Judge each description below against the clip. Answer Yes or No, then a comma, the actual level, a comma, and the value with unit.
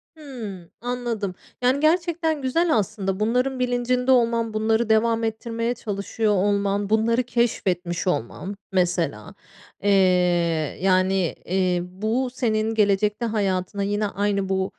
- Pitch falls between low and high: No, high, 215 Hz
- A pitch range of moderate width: Yes, average, 3.8 semitones